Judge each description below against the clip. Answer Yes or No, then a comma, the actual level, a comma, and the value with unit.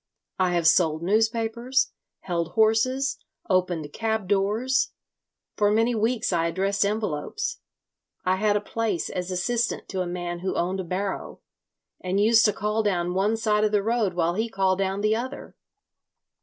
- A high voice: Yes, high, 205 Hz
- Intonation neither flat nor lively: Yes, average, 3.5 semitones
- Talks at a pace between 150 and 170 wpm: Yes, average, 160 wpm